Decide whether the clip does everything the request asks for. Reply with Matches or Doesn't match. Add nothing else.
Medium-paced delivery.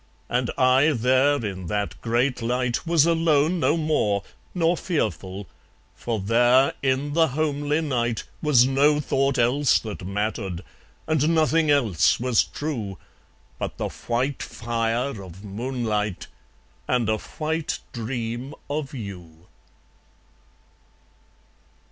Doesn't match